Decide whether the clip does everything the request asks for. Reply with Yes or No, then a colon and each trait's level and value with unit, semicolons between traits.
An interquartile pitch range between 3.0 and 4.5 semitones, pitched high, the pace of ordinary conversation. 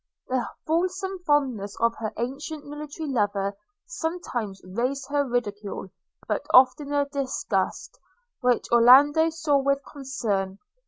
No: average, 4.1 semitones; very high, 270 Hz; slow, 110 wpm